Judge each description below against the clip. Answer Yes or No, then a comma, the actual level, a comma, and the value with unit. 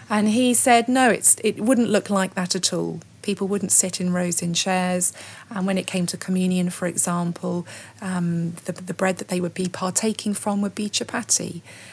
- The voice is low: No, medium, 185 Hz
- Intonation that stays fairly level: Yes, narrow, 2.3 semitones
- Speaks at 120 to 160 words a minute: No, average, 200 wpm